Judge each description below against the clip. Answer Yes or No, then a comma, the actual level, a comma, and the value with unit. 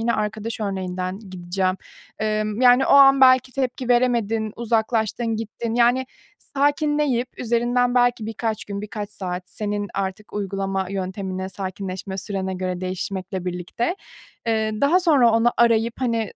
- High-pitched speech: Yes, high, 220 Hz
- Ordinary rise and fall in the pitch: Yes, average, 4.0 semitones